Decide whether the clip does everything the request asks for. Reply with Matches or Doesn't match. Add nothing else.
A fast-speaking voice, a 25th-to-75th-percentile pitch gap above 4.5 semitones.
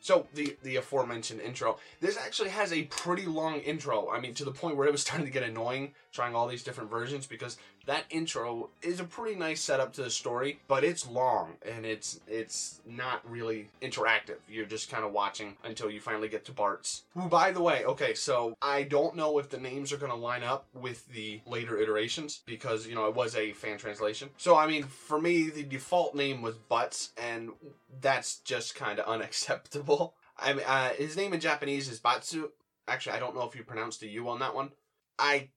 Matches